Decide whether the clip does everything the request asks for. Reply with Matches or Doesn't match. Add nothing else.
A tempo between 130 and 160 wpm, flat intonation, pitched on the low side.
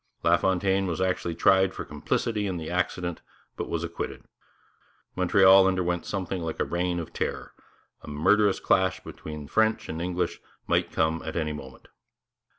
Matches